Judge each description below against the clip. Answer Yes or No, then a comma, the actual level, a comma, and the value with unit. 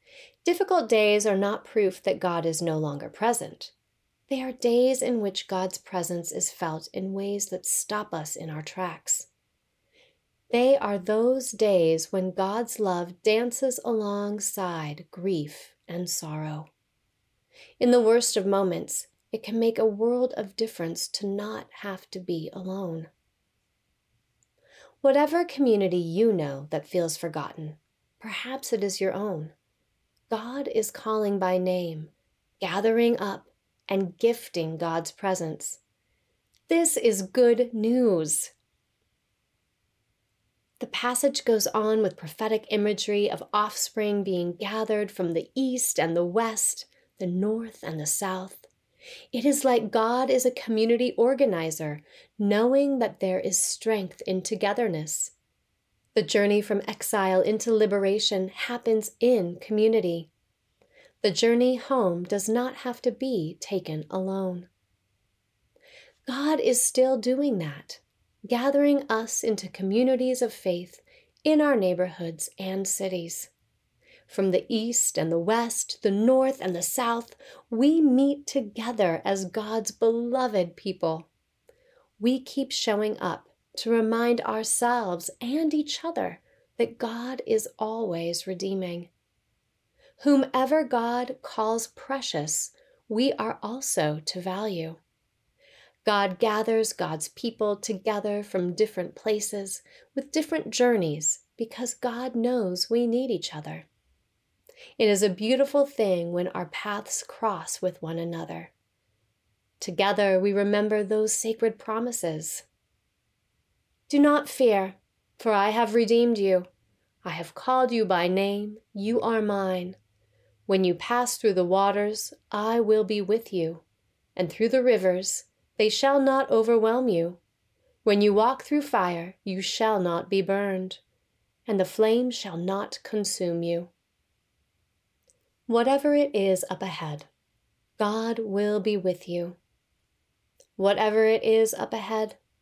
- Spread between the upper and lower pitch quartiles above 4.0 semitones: Yes, average, 4.8 semitones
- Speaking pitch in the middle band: No, high, 210 Hz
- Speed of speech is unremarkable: No, slow, 130 wpm